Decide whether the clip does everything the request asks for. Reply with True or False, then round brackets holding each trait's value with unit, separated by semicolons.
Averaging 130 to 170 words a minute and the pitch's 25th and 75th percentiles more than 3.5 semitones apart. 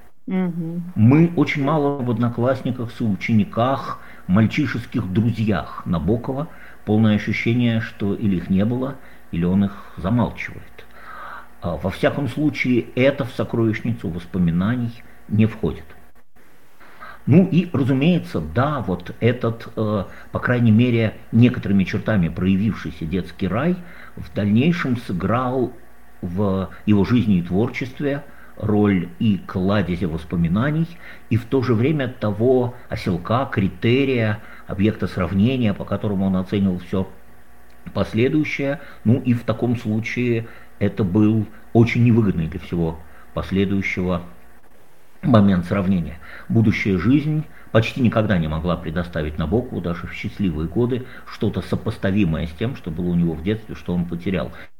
False (120 wpm; 4.6 semitones)